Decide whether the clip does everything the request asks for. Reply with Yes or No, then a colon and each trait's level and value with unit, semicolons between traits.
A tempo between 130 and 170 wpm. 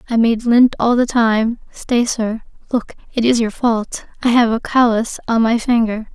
No: average, 195 wpm